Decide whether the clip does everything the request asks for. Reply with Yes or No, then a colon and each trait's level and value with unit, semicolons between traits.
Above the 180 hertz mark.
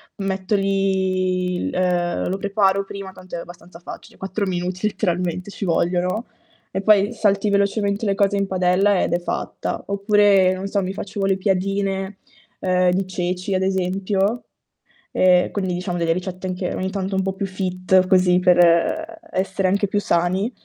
Yes: high, 190 Hz